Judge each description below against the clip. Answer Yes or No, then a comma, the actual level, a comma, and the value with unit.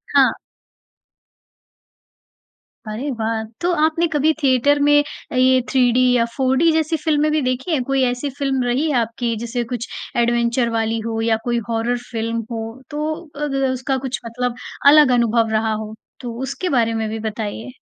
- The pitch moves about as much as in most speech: Yes, average, 3.8 semitones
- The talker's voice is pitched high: Yes, high, 245 Hz